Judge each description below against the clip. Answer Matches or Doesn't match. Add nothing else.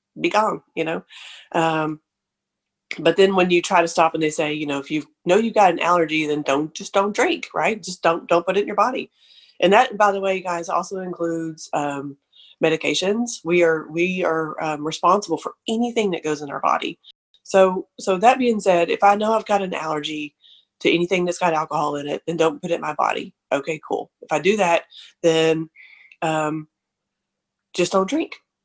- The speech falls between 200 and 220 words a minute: Matches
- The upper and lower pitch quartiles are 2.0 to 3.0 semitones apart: Doesn't match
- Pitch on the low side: Doesn't match